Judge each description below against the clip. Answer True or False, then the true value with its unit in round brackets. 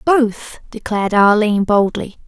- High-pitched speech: True (215 Hz)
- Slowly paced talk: True (105 wpm)